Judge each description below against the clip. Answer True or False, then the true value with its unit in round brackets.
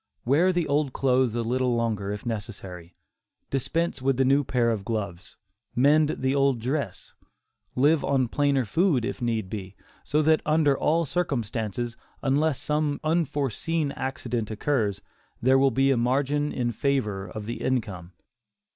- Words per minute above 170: False (150 wpm)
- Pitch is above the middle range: False (130 Hz)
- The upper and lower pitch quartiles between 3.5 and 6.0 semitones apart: True (4.2 semitones)